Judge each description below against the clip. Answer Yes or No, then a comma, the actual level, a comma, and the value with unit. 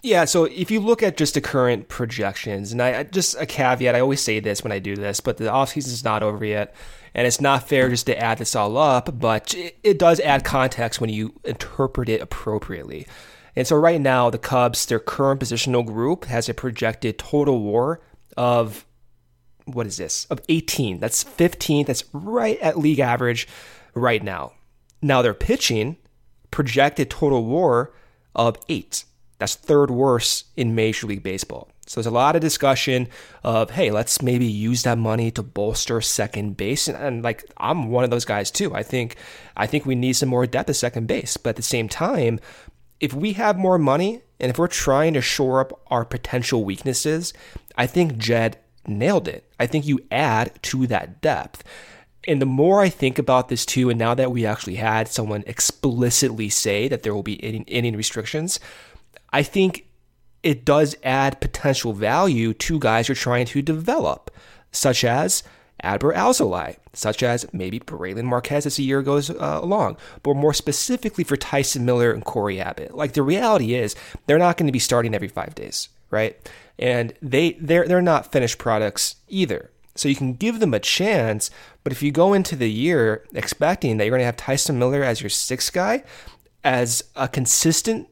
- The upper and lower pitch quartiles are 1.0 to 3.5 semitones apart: No, average, 4.4 semitones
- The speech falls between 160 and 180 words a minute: No, average, 190 wpm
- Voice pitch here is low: Yes, low, 125 Hz